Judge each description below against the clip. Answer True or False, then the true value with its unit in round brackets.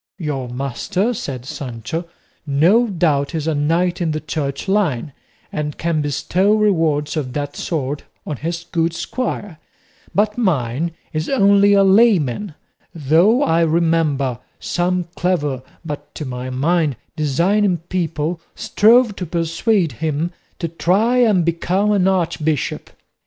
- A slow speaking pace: True (130 wpm)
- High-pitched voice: False (165 Hz)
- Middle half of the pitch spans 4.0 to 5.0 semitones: True (4.4 semitones)